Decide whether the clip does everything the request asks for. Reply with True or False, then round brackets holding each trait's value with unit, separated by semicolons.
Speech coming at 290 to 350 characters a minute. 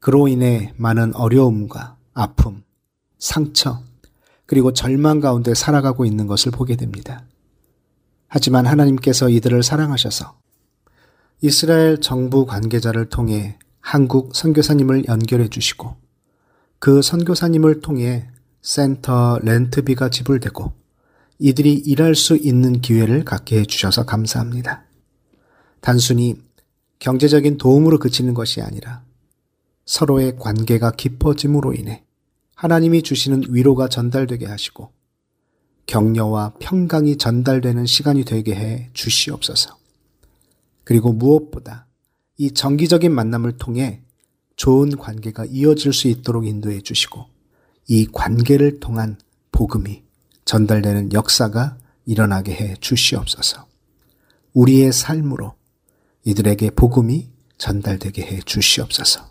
False (275 characters per minute)